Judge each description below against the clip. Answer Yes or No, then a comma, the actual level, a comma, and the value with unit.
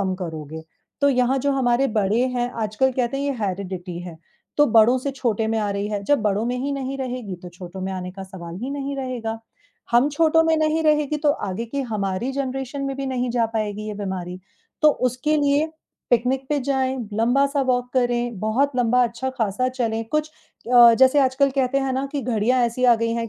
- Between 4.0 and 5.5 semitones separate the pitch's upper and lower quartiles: Yes, average, 4.3 semitones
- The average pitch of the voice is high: Yes, high, 245 Hz